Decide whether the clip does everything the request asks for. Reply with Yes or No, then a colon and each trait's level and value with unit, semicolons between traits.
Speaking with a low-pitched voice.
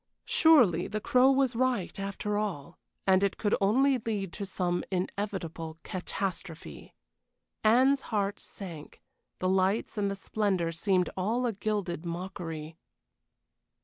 No: high, 195 Hz